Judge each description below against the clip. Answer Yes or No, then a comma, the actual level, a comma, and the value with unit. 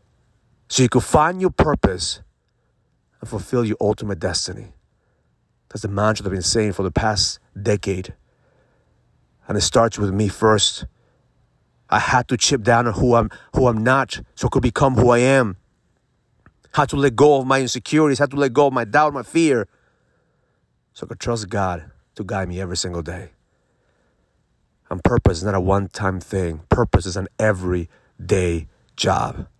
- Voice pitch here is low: Yes, low, 110 Hz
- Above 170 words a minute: Yes, average, 180 wpm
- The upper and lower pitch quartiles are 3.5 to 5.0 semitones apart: Yes, average, 4.6 semitones